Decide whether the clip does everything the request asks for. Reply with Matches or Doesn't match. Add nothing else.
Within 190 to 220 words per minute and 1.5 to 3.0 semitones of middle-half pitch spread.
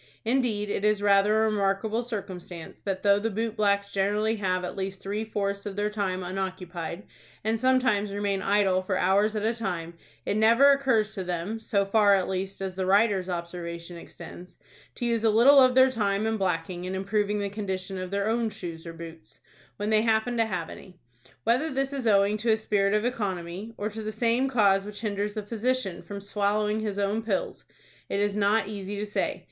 Matches